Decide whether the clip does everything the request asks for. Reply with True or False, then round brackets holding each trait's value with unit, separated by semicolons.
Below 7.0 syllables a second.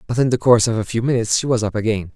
False (8.0 syllables/s)